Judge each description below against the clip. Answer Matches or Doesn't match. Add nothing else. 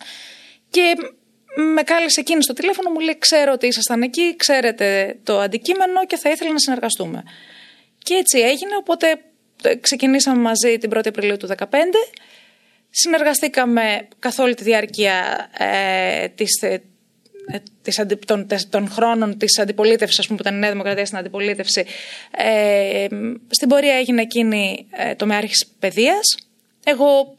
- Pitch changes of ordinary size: Doesn't match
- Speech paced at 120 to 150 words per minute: Matches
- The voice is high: Matches